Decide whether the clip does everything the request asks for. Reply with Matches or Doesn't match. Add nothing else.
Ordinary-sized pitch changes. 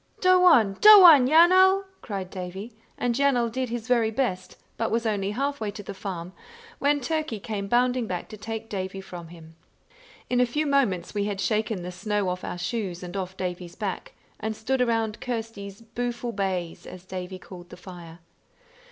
Matches